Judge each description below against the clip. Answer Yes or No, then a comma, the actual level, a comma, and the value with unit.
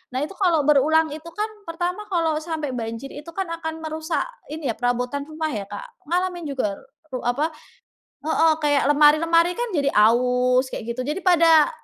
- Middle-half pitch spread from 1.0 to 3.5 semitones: No, average, 4.4 semitones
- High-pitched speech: Yes, very high, 310 Hz